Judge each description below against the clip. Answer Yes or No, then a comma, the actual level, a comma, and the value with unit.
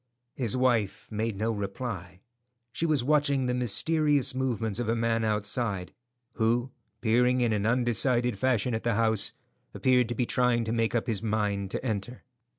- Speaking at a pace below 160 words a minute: No, average, 165 wpm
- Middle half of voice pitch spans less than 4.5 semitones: Yes, narrow, 2.5 semitones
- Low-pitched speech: Yes, low, 115 Hz